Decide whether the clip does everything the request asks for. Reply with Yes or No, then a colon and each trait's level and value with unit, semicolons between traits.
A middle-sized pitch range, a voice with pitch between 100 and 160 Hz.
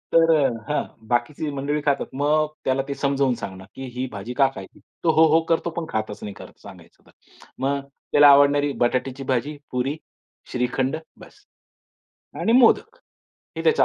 Yes: average, 3.2 semitones; medium, 140 Hz